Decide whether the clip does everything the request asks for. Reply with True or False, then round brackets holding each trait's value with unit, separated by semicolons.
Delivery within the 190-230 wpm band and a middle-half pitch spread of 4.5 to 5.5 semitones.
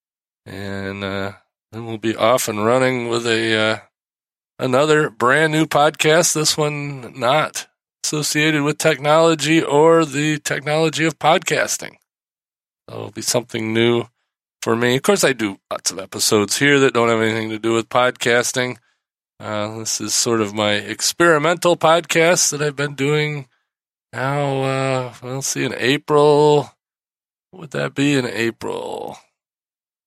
False (150 wpm; 5.1 semitones)